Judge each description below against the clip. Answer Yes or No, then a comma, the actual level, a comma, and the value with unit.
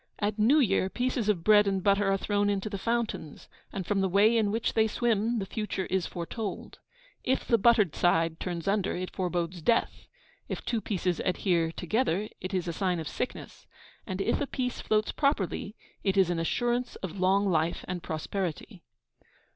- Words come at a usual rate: Yes, average, 185 wpm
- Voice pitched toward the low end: No, high, 195 Hz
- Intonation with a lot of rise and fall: No, average, 3.4 semitones